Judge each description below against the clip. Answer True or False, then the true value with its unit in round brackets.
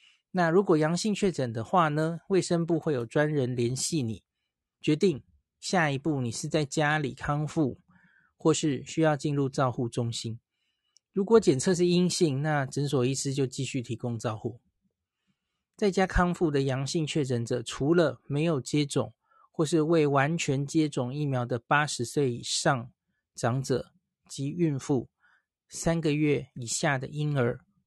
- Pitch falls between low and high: True (150 Hz)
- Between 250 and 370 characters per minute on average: False (225 characters per minute)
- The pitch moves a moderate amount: True (4.4 semitones)